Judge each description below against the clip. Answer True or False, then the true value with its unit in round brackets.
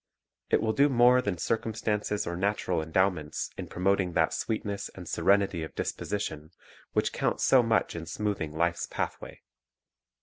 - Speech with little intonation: False (4.3 semitones)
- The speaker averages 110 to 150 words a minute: True (145 wpm)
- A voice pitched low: True (100 Hz)